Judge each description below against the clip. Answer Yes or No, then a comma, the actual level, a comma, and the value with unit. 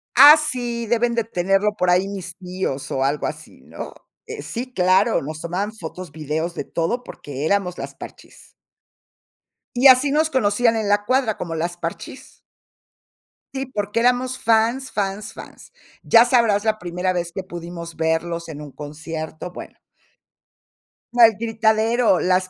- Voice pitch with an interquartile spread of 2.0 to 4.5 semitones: No, wide, 5.4 semitones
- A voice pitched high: Yes, high, 200 Hz